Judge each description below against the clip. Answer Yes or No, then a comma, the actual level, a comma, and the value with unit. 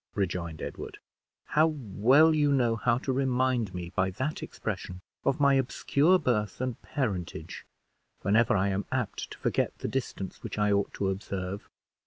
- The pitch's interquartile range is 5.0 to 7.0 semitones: Yes, wide, 5.5 semitones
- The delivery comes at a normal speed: Yes, average, 160 wpm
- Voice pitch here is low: Yes, low, 115 Hz